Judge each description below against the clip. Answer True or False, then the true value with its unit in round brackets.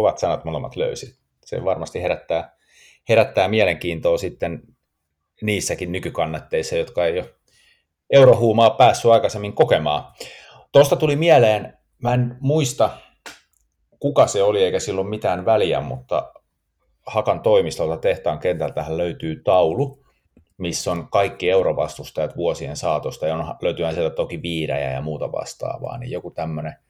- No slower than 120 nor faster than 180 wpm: True (125 wpm)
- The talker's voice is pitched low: False (175 Hz)